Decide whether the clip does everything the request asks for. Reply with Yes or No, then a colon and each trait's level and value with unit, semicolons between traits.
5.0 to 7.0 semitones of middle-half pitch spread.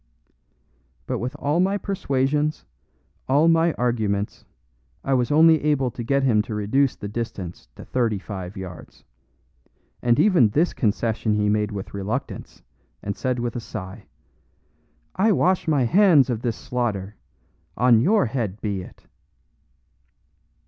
Yes: wide, 5.6 semitones